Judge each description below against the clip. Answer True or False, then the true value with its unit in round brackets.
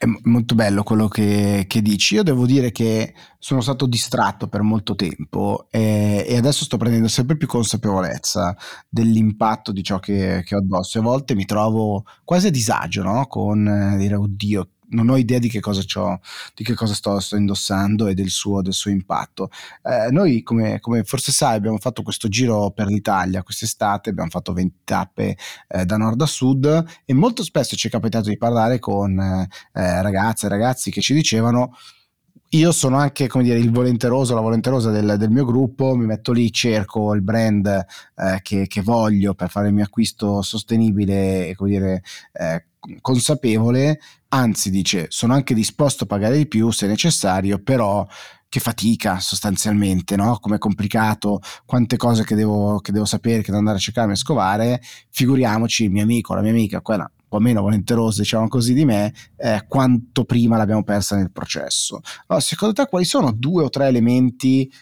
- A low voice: True (110 Hz)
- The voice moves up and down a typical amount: True (3.3 semitones)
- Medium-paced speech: False (185 wpm)